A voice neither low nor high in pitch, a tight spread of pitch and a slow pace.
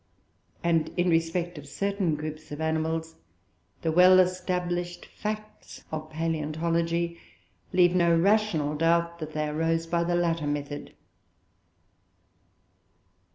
Yes: medium, 165 Hz; narrow, 1.9 semitones; slow, 110 wpm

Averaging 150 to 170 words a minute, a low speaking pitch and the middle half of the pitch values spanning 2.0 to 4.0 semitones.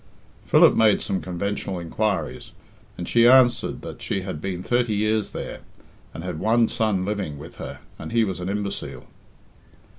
Yes: average, 160 wpm; low, 100 Hz; average, 3.2 semitones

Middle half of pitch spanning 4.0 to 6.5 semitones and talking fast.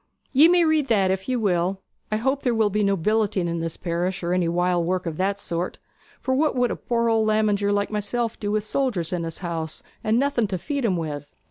Yes: average, 4.7 semitones; fast, 235 wpm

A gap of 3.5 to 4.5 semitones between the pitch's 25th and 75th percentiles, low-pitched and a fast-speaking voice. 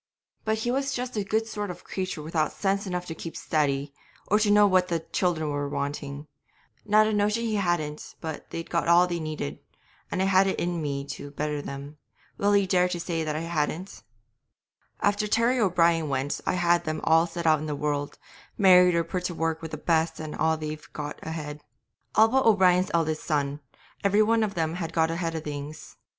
No: average, 4.2 semitones; medium, 170 Hz; fast, 210 wpm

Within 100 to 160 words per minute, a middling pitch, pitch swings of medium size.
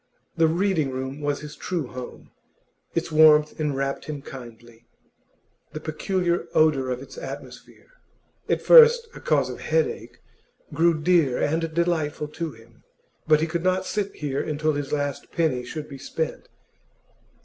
Yes: average, 150 wpm; medium, 155 Hz; average, 3.5 semitones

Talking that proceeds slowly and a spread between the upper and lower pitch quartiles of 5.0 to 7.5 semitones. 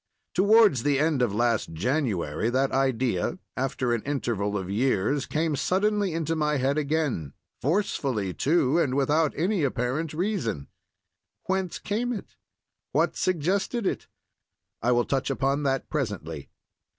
Yes: slow, 130 wpm; average, 5.3 semitones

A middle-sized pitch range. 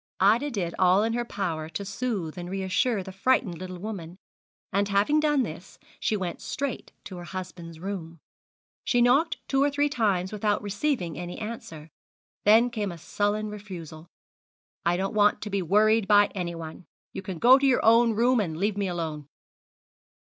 Yes: average, 4.3 semitones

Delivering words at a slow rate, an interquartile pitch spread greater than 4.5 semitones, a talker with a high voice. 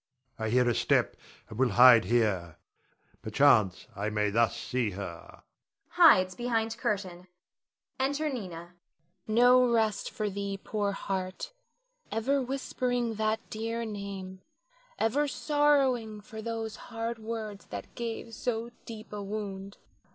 Yes: slow, 130 wpm; average, 5.3 semitones; high, 215 Hz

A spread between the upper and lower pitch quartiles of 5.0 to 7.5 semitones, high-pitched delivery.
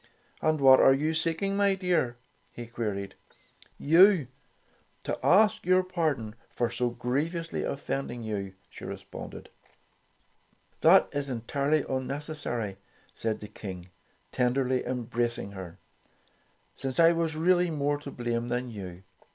No: wide, 5.4 semitones; low, 130 Hz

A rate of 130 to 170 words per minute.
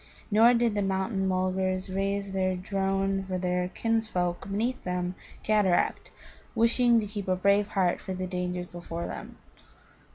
Yes: average, 150 wpm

